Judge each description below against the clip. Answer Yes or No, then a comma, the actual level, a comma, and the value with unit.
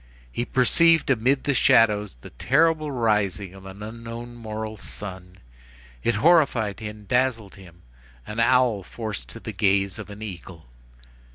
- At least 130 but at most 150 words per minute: Yes, average, 145 wpm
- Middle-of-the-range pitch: No, low, 110 Hz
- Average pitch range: Yes, average, 3.9 semitones